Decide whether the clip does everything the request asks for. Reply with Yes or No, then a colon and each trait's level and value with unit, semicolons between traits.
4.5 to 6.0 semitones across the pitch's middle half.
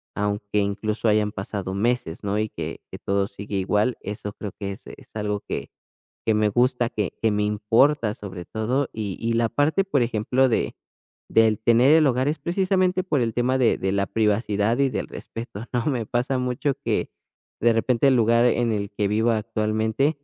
No: average, 3.3 semitones